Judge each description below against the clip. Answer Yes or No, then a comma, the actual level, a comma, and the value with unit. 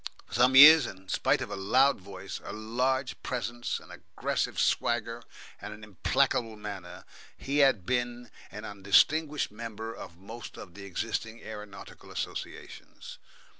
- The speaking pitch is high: No, low, 115 Hz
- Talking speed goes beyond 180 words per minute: No, average, 140 wpm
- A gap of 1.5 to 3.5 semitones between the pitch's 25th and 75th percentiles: No, average, 4.1 semitones